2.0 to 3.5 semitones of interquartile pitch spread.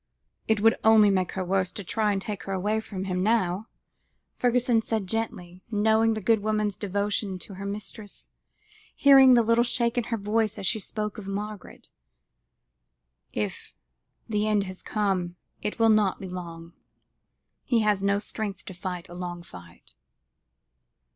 Yes: average, 2.8 semitones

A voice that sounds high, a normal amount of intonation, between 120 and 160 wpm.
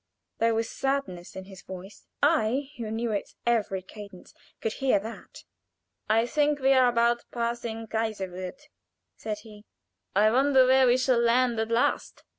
Yes: high, 230 Hz; average, 3.3 semitones; average, 155 wpm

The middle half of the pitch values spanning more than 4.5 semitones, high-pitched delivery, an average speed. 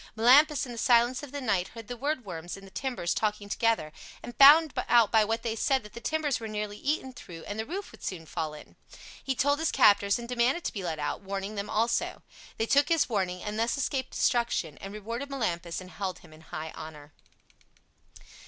No: average, 5.2 semitones; high, 225 Hz; fast, 215 wpm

